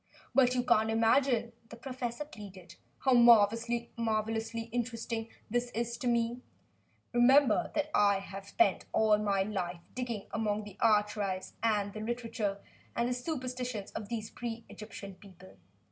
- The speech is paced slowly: No, average, 145 wpm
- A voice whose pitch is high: Yes, high, 225 Hz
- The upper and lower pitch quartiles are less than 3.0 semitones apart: Yes, narrow, 2.6 semitones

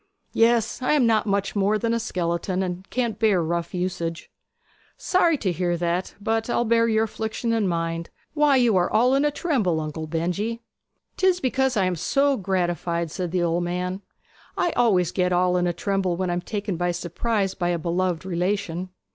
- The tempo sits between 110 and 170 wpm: No, average, 190 wpm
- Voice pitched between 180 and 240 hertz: Yes, high, 190 Hz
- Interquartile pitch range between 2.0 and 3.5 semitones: No, average, 4.7 semitones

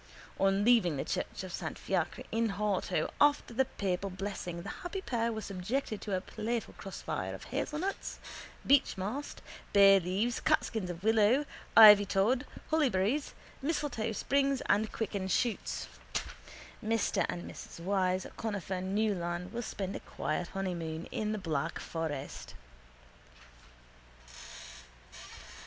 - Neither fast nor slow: No, slow, 120 wpm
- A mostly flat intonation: No, average, 3.9 semitones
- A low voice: No, high, 205 Hz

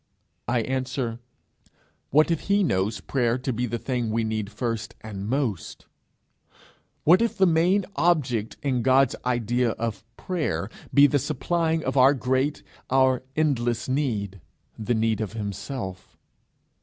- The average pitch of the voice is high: No, low, 125 Hz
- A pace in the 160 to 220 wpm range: No, average, 140 wpm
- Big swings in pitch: No, average, 4.5 semitones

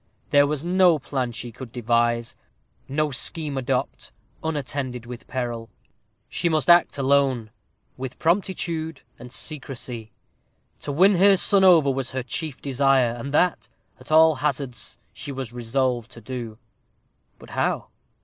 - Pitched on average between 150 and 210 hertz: No, low, 135 Hz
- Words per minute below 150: Yes, average, 140 wpm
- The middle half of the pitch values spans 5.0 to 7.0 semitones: No, average, 4.3 semitones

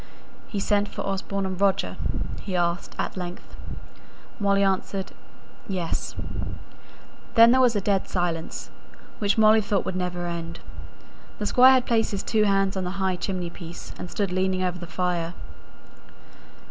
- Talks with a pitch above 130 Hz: Yes, high, 190 Hz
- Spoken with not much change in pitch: Yes, narrow, 2.2 semitones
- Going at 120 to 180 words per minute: Yes, average, 155 wpm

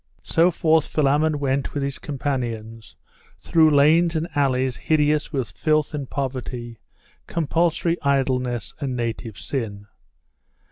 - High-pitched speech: No, medium, 140 Hz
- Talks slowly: Yes, slow, 120 wpm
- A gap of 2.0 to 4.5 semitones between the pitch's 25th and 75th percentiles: Yes, average, 3.6 semitones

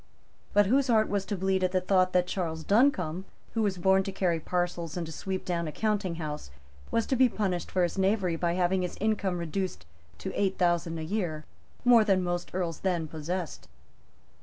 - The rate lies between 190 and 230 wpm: Yes, average, 200 wpm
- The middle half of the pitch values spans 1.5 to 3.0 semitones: Yes, narrow, 2.6 semitones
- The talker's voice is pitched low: No, medium, 185 Hz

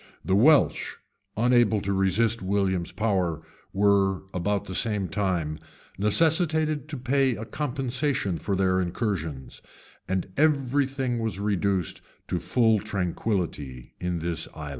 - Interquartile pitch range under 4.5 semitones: No, average, 5.1 semitones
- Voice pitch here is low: Yes, low, 100 Hz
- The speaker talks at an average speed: No, slow, 125 wpm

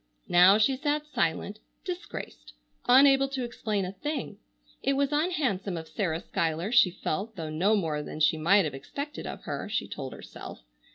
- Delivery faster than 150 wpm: Yes, average, 170 wpm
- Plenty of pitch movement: Yes, wide, 8.6 semitones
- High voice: Yes, high, 205 Hz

